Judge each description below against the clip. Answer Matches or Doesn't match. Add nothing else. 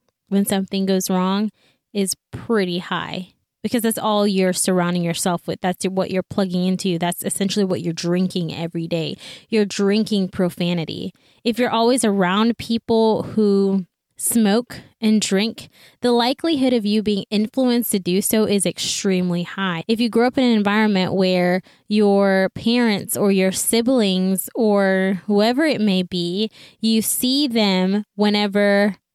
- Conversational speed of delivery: Matches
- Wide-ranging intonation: Doesn't match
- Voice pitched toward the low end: Doesn't match